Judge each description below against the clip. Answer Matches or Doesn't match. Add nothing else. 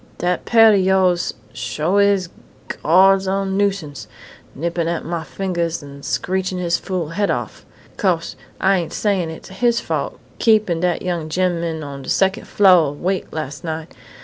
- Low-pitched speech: Doesn't match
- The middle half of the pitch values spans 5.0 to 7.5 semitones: Doesn't match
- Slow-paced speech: Doesn't match